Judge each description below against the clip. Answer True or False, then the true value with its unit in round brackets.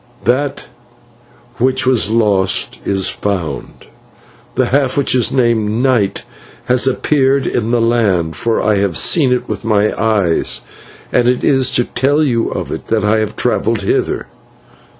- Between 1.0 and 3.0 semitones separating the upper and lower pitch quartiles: False (3.9 semitones)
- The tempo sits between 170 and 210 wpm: False (150 wpm)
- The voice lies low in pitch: True (115 Hz)